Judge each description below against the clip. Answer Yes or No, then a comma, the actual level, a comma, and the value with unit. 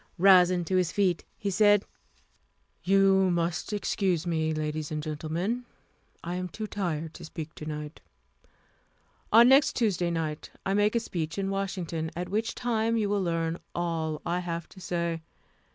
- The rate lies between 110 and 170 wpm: Yes, average, 160 wpm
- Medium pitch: Yes, medium, 180 Hz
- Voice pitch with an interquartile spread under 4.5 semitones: Yes, average, 3.4 semitones